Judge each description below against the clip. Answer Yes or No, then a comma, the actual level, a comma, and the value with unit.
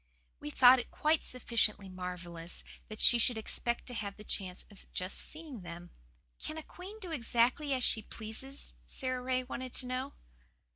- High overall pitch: Yes, high, 240 Hz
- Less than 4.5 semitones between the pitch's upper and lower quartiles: No, average, 4.8 semitones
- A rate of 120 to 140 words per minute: No, average, 175 wpm